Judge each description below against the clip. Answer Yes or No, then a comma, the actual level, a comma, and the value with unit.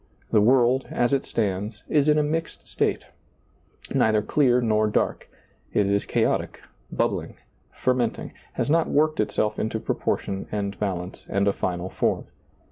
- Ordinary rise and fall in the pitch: Yes, average, 4.7 semitones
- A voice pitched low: Yes, low, 110 Hz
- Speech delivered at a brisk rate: No, average, 155 wpm